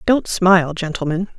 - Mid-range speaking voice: Yes, medium, 180 Hz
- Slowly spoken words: Yes, slow, 130 wpm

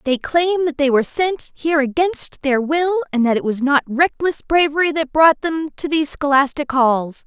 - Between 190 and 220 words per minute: Yes, average, 200 wpm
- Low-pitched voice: No, very high, 295 Hz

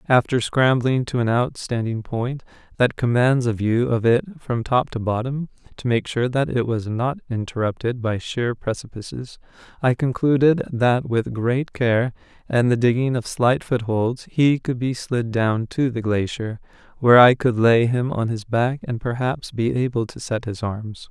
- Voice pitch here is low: Yes, low, 120 Hz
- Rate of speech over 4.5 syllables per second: No, 4.4 syllables/s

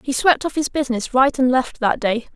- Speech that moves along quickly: Yes, fast, 255 wpm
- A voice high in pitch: Yes, very high, 260 Hz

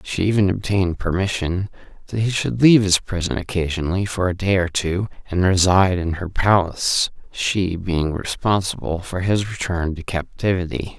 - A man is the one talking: Yes, male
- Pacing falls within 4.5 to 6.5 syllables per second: Yes, 5.0 syllables/s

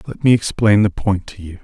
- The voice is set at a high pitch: No, low, 100 Hz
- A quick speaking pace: Yes, fast, 255 wpm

